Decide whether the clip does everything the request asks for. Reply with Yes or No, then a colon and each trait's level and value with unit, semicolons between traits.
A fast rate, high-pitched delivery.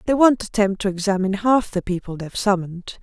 Yes: fast, 220 wpm; high, 200 Hz